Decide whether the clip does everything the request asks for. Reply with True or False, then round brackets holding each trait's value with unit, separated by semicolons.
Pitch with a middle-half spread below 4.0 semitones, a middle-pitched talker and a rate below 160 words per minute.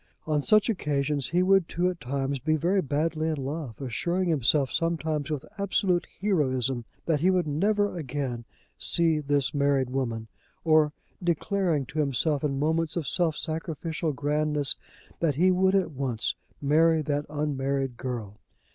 True (3.5 semitones; 150 Hz; 150 wpm)